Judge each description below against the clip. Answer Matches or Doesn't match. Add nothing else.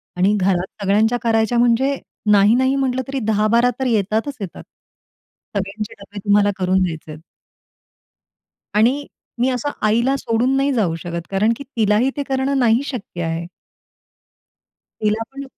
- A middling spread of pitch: Matches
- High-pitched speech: Matches